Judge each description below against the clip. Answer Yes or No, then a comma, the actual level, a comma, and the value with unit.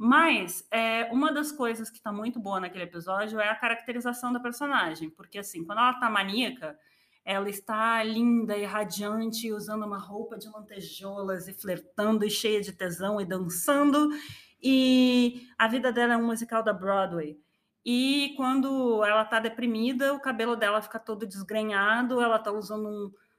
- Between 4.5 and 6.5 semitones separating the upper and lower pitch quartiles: No, average, 3.2 semitones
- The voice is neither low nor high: No, high, 225 Hz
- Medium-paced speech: Yes, average, 165 wpm